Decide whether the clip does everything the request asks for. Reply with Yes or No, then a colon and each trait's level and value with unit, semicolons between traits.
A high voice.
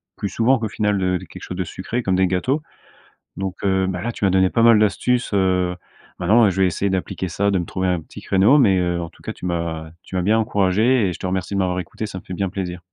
No: very low, 95 Hz